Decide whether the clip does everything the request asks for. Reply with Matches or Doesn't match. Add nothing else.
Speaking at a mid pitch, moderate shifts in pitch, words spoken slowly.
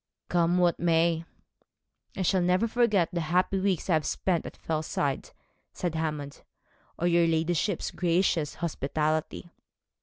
Doesn't match